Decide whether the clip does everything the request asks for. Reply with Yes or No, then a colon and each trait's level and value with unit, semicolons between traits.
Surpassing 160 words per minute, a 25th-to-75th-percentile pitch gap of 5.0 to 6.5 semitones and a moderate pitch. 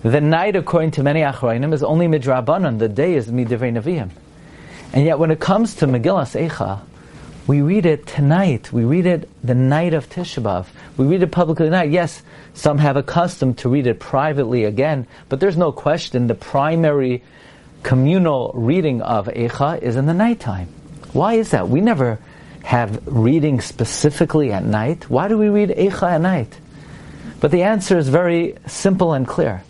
Yes: average, 180 wpm; average, 5.3 semitones; medium, 150 Hz